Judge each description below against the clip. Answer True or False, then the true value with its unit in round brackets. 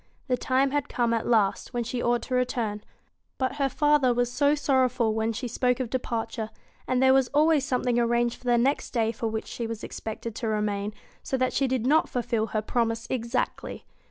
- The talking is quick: True (210 wpm)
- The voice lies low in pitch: False (240 Hz)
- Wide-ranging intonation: False (2.4 semitones)